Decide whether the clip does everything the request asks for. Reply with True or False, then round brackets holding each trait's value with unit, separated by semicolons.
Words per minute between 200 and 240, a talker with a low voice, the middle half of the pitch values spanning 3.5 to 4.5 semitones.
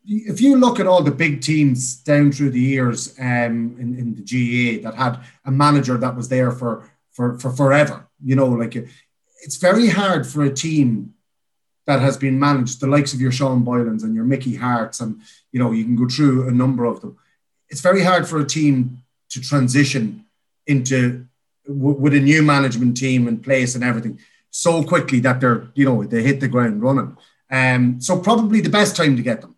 False (205 wpm; 130 Hz; 2.9 semitones)